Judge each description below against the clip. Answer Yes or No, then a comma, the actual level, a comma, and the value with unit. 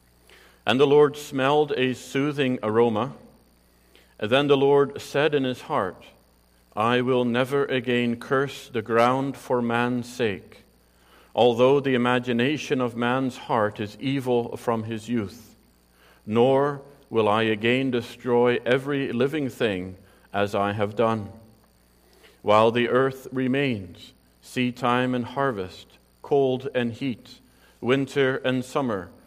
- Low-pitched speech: Yes, low, 120 Hz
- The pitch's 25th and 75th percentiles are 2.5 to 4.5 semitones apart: Yes, average, 3.6 semitones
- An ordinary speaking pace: No, slow, 125 wpm